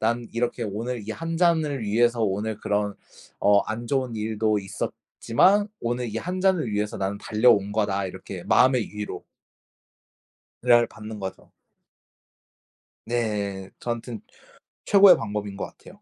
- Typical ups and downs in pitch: Yes, average, 3.1 semitones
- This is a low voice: Yes, low, 110 Hz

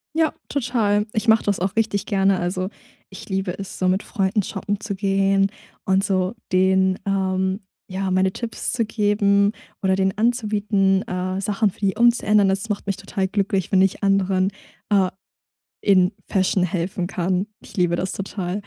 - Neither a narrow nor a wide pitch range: No, narrow, 1.5 semitones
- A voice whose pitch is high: Yes, high, 195 Hz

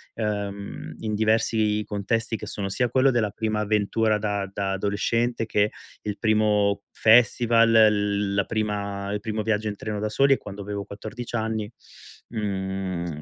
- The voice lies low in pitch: Yes, low, 105 Hz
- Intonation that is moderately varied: No, narrow, 1.8 semitones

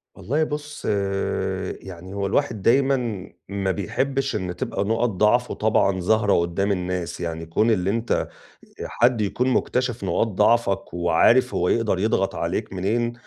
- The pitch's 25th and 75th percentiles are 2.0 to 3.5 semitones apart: No, average, 4.2 semitones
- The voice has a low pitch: Yes, low, 105 Hz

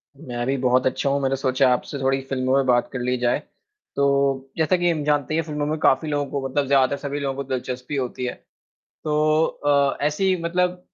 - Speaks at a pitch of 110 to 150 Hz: Yes, medium, 140 Hz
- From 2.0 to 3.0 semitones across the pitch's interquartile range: Yes, narrow, 2.5 semitones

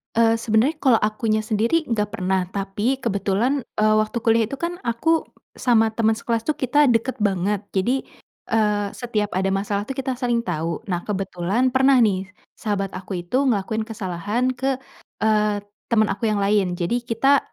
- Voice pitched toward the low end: No, high, 220 Hz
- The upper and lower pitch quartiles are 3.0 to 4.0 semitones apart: Yes, average, 3.4 semitones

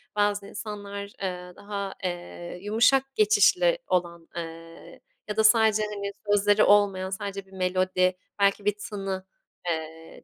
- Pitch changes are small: Yes, narrow, 2.2 semitones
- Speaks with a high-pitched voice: Yes, high, 200 Hz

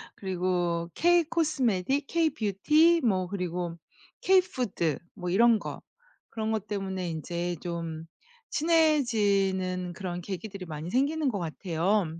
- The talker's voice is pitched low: No, high, 195 Hz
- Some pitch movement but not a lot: No, wide, 6.6 semitones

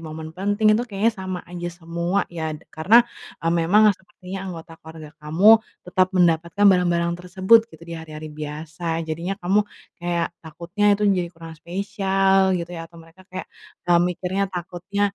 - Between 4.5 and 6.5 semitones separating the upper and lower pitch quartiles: No, average, 2.8 semitones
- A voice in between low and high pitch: Yes, medium, 175 Hz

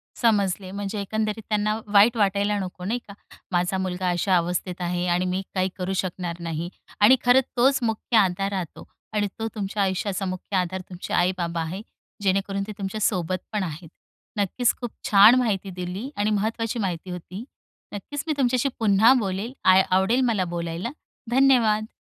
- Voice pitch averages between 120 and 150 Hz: No, high, 195 Hz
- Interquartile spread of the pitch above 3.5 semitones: No, average, 3.0 semitones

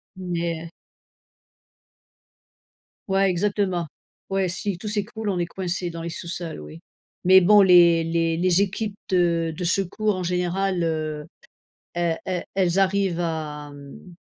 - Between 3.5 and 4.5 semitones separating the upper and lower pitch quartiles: No, narrow, 2.5 semitones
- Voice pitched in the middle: Yes, medium, 175 Hz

